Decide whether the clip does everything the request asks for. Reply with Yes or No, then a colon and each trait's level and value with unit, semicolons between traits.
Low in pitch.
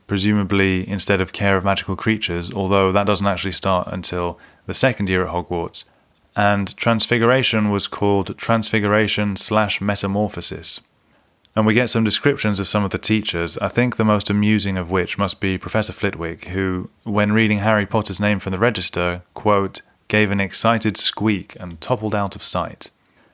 Yes: low, 100 Hz